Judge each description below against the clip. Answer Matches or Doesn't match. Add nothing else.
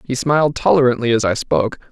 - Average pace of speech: Matches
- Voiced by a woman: Doesn't match